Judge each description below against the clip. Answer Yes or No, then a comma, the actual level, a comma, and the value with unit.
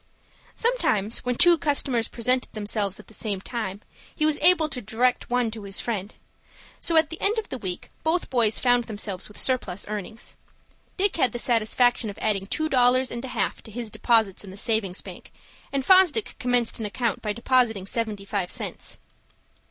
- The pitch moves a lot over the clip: No, average, 3.7 semitones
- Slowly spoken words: No, average, 185 wpm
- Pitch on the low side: No, high, 235 Hz